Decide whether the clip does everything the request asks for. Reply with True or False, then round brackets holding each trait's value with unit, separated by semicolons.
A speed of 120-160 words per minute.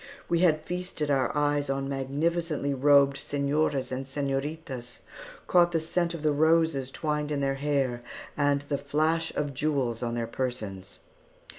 True (150 wpm)